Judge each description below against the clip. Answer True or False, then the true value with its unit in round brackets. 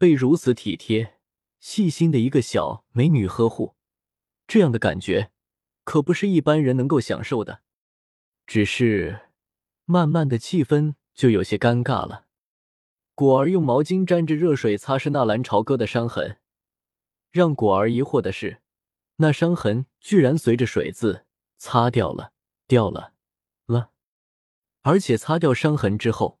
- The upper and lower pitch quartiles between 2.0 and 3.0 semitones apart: False (5.6 semitones)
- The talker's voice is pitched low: True (130 Hz)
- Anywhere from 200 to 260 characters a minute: True (210 characters per minute)